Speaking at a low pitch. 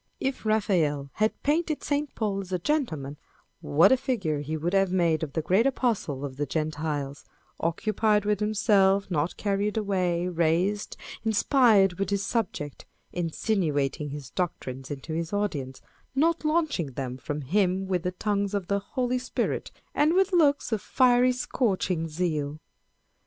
No: high, 190 Hz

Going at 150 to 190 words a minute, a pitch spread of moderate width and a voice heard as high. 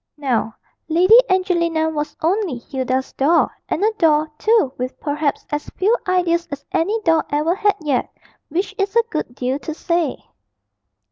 Yes: average, 155 wpm; average, 4.3 semitones; very high, 320 Hz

